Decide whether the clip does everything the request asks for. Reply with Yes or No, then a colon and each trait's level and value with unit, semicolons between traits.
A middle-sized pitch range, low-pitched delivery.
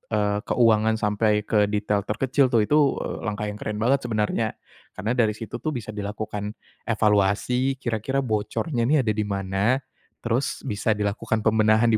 No: narrow, 2.3 semitones; low, 110 Hz